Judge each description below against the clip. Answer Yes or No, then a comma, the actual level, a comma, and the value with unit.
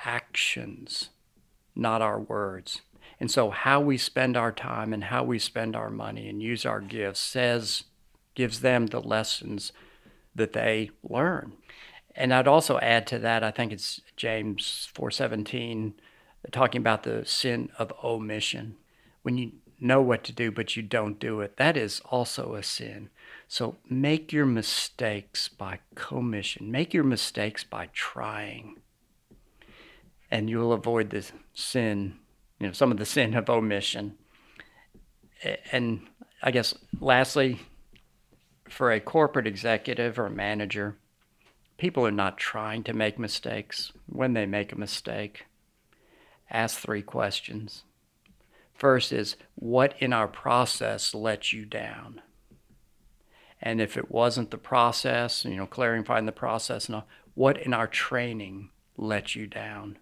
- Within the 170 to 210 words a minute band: No, average, 140 wpm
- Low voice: Yes, low, 115 Hz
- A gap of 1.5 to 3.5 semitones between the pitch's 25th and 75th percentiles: Yes, average, 2.9 semitones